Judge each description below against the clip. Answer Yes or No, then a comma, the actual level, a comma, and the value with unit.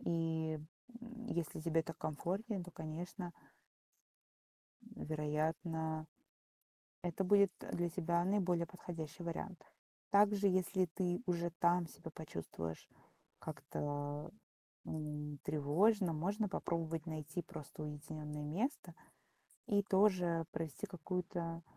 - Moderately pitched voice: Yes, medium, 170 Hz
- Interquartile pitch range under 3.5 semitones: Yes, average, 2.9 semitones